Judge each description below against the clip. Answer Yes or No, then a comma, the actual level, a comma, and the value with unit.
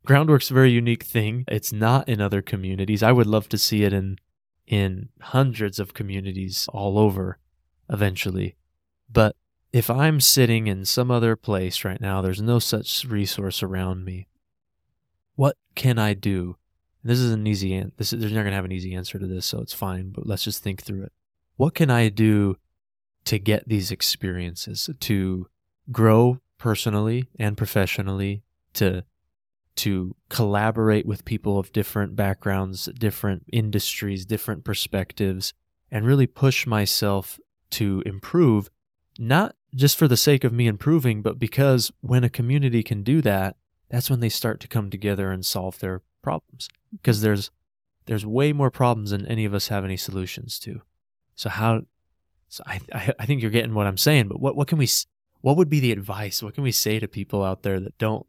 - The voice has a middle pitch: No, low, 105 Hz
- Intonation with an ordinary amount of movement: Yes, average, 3.8 semitones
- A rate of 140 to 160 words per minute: No, average, 175 wpm